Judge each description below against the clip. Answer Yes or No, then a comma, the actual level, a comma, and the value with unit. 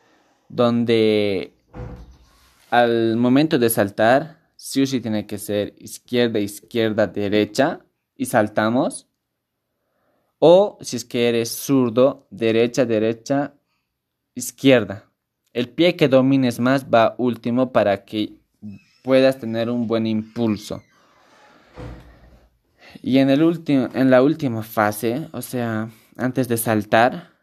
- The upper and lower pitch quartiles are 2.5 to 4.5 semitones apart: Yes, average, 3.4 semitones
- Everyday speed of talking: No, slow, 110 wpm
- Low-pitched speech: Yes, low, 120 Hz